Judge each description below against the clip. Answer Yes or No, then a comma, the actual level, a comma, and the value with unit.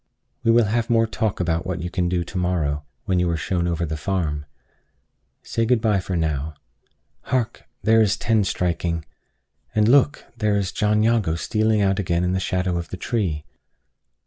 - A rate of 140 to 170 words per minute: No, average, 180 wpm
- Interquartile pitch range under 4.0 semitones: No, average, 4.3 semitones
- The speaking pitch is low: Yes, very low, 95 Hz